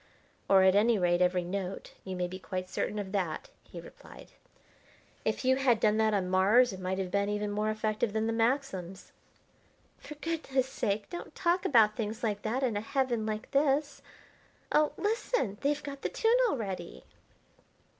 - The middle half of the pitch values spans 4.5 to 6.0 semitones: Yes, wide, 5.5 semitones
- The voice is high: Yes, high, 215 Hz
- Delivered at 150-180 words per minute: Yes, average, 175 wpm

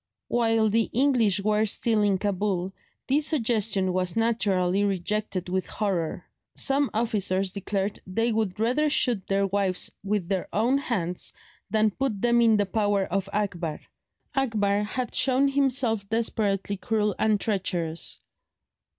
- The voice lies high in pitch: Yes, high, 210 Hz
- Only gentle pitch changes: No, average, 3.0 semitones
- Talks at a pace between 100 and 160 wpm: Yes, slow, 135 wpm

